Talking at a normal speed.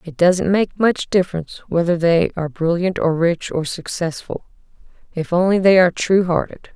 Yes: average, 170 wpm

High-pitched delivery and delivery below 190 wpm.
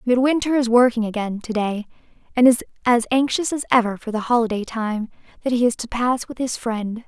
No: high, 235 Hz; fast, 205 wpm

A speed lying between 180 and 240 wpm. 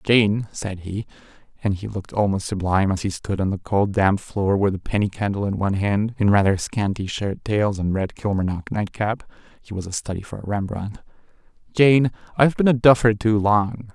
Yes: average, 200 wpm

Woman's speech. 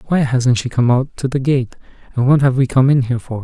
No: male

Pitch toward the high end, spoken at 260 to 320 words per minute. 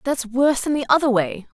No: very high, 250 Hz; fast, 225 wpm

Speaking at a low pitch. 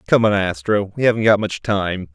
Yes: low, 100 Hz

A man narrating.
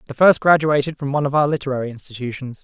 Yes: male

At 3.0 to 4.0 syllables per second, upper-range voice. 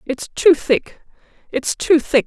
Yes: 3.5 syllables/s; very high, 295 Hz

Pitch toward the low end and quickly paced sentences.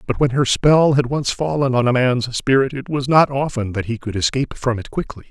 Yes: low, 130 Hz; fast, 250 wpm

